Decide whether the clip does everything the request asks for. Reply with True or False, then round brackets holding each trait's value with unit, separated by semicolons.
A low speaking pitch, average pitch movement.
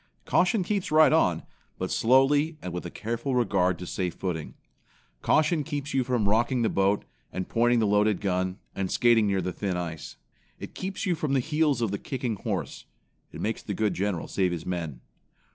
False (110 Hz; 6.6 semitones)